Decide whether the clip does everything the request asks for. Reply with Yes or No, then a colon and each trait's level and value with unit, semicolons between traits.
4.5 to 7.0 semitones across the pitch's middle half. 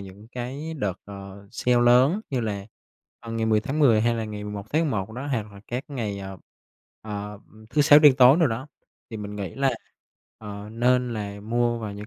No: average, 3.7 semitones